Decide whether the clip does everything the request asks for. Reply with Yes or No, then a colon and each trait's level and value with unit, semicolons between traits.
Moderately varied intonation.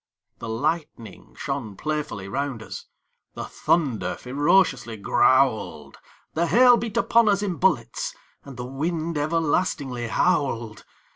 No: wide, 5.9 semitones